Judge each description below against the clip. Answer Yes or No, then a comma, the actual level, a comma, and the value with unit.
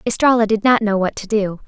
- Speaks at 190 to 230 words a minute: No, fast, 250 wpm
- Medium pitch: No, high, 215 Hz